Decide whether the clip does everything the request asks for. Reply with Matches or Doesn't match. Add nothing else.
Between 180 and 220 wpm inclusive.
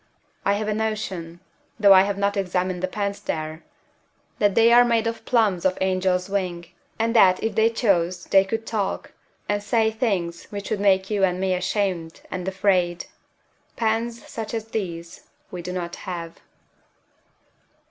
Doesn't match